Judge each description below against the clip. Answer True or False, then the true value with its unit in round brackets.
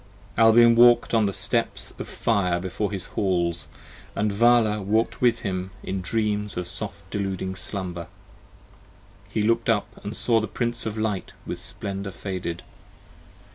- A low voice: True (105 Hz)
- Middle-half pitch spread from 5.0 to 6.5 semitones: False (3.3 semitones)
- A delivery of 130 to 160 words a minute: True (150 wpm)